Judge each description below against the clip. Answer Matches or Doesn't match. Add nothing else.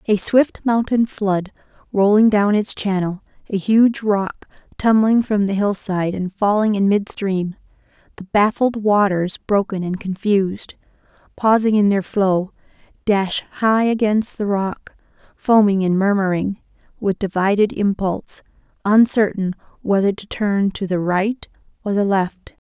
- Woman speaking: Matches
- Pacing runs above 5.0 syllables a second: Doesn't match